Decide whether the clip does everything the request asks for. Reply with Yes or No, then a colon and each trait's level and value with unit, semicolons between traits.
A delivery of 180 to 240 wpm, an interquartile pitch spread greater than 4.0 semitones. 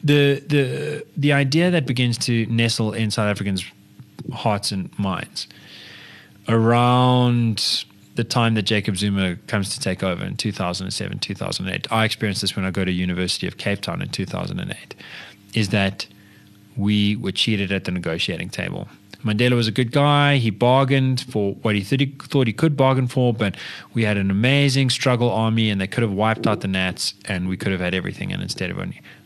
Yes: fast, 205 wpm; average, 4.4 semitones